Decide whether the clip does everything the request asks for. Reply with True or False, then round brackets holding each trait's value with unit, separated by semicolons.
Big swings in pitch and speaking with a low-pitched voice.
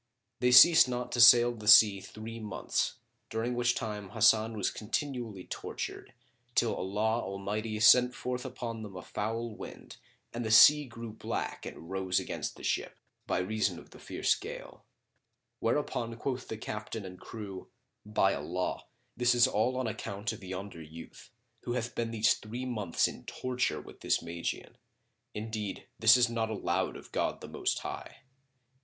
False (2.7 semitones; 110 Hz)